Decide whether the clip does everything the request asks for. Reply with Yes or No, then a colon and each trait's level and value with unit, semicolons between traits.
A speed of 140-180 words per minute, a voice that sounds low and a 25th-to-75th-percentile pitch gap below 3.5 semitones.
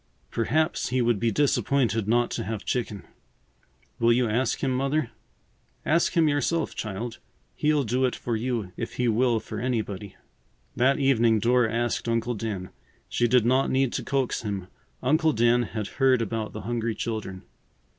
Yes: average, 165 wpm; low, 120 Hz; average, 2.8 semitones